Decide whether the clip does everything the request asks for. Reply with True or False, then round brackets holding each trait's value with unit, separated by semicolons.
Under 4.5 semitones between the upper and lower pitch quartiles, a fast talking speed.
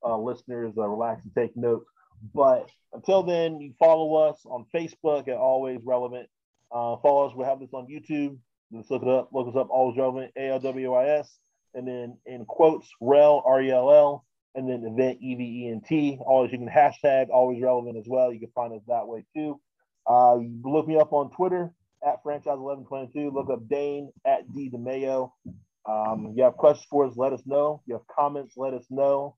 True (2.9 semitones; 220 wpm)